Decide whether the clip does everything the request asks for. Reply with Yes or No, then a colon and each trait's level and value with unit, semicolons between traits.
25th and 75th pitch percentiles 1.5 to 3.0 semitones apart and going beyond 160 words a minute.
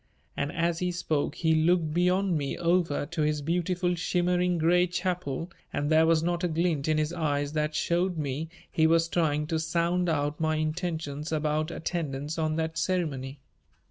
Yes: narrow, 2.4 semitones; average, 175 wpm